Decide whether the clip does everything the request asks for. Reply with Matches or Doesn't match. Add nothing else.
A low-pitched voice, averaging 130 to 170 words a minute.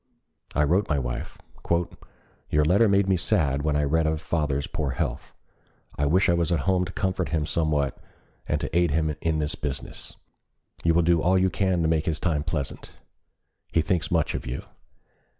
Doesn't match